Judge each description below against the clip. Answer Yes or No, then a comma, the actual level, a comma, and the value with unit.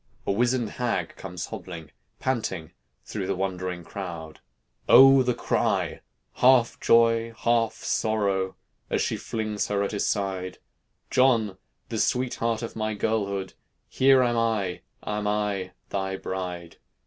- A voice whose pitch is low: Yes, low, 105 Hz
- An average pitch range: Yes, average, 3.5 semitones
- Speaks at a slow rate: Yes, slow, 130 wpm